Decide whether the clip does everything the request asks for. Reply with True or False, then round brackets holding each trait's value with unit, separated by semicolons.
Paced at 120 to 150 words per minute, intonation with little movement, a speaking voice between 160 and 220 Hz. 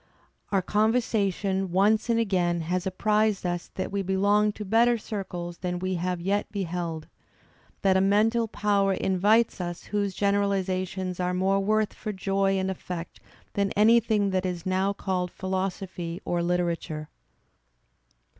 True (140 wpm; 2.3 semitones; 190 Hz)